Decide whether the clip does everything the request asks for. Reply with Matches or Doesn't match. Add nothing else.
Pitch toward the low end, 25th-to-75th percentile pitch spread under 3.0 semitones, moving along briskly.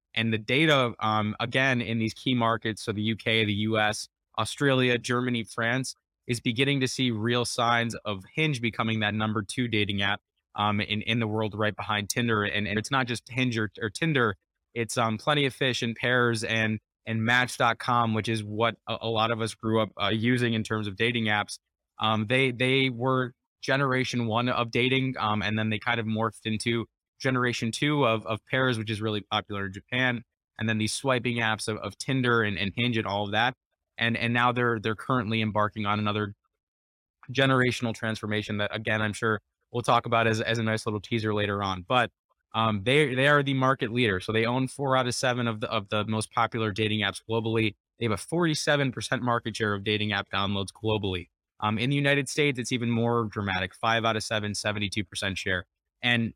Matches